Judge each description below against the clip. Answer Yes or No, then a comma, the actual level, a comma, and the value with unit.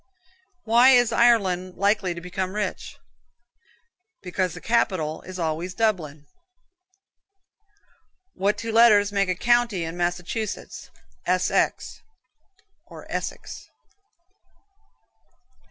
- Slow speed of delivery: Yes, slow, 95 wpm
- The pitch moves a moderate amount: Yes, average, 4.0 semitones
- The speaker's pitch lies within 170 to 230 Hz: Yes, high, 190 Hz